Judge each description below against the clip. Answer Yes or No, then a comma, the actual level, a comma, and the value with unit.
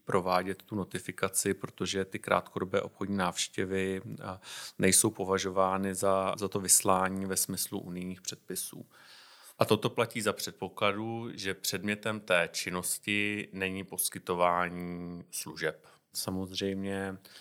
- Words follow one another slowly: Yes, slow, 105 wpm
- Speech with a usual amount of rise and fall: No, narrow, 1.0 semitones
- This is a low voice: Yes, very low, 95 Hz